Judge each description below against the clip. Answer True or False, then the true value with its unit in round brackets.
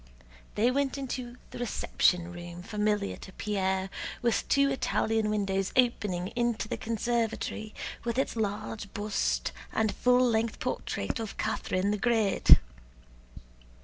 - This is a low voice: False (215 Hz)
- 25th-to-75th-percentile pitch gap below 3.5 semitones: True (3.1 semitones)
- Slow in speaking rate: True (125 wpm)